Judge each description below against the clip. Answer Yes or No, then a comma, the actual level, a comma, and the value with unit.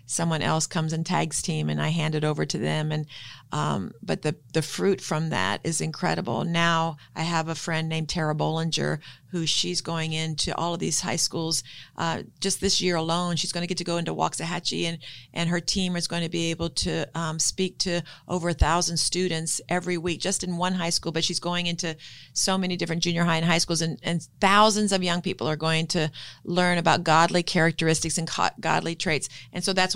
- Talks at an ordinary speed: No, fast, 215 wpm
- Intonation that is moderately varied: No, narrow, 1.8 semitones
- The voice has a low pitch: No, medium, 165 Hz